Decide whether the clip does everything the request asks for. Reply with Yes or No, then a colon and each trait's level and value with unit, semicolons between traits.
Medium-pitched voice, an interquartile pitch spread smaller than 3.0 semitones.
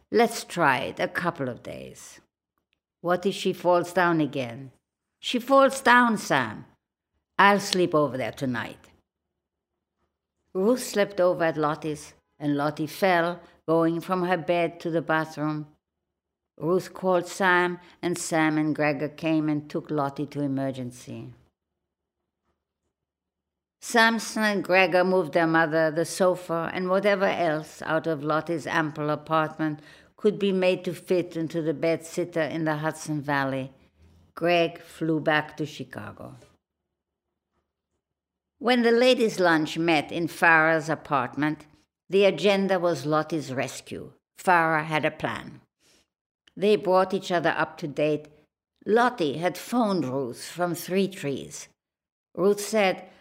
No: medium, 160 Hz; average, 4.2 semitones